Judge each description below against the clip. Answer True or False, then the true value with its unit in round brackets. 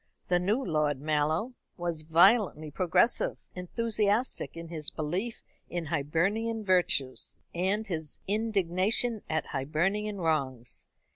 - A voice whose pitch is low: False (175 Hz)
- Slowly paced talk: True (110 wpm)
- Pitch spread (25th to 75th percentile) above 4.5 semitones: True (5.2 semitones)